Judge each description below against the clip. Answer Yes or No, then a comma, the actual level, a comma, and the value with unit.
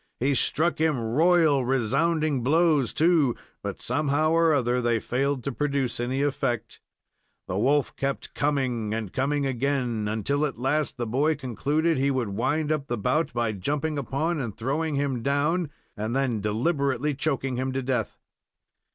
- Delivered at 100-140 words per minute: No, average, 160 wpm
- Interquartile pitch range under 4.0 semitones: Yes, average, 3.6 semitones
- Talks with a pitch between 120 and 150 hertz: Yes, low, 135 Hz